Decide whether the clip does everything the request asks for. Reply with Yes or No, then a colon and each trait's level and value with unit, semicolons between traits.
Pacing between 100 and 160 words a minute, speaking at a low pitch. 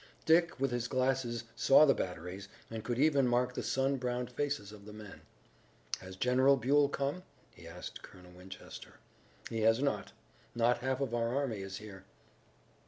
No: average, 170 wpm; low, 120 Hz